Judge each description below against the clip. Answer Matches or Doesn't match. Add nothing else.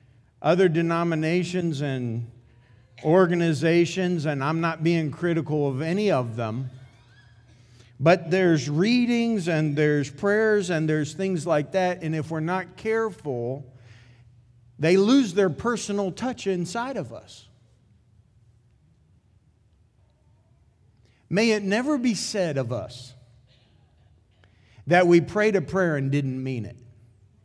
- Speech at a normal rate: Doesn't match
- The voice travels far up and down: Matches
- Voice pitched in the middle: Matches